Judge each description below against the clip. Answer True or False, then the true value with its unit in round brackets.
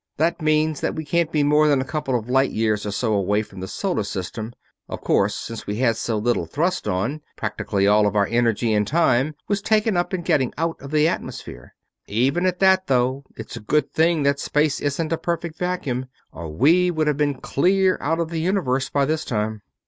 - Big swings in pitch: True (6.4 semitones)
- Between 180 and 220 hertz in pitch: False (140 Hz)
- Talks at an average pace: False (215 wpm)